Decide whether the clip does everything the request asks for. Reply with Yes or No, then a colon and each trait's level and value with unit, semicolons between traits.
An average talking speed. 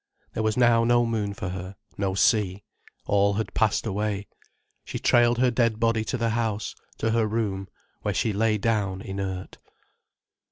Yes: average, 165 wpm